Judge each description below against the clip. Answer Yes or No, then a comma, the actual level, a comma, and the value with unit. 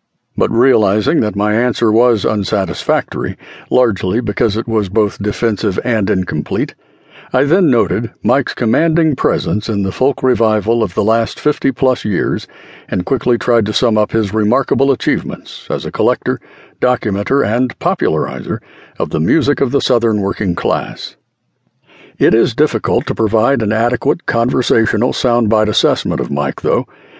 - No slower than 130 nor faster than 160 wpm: Yes, average, 150 wpm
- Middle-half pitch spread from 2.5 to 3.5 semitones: Yes, average, 2.8 semitones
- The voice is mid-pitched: No, low, 115 Hz